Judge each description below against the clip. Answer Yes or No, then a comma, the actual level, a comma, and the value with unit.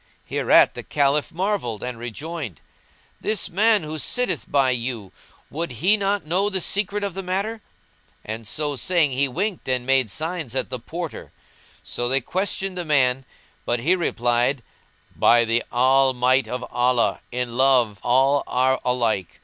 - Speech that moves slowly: No, average, 155 wpm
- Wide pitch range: Yes, wide, 6.4 semitones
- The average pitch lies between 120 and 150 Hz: Yes, low, 135 Hz